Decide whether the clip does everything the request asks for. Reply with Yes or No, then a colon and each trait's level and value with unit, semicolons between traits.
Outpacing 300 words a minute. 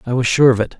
Yes: fast, 380 wpm